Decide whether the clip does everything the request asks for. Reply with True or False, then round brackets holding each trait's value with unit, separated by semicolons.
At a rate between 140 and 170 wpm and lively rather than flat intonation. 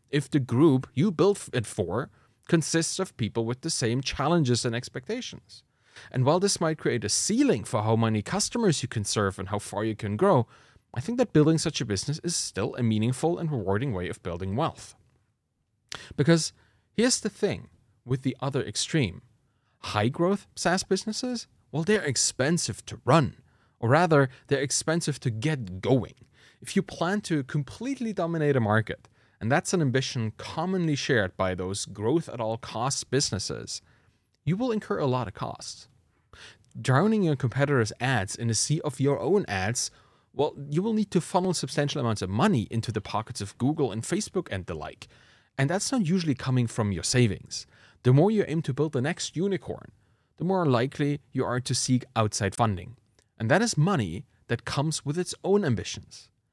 False (180 wpm; 6.5 semitones)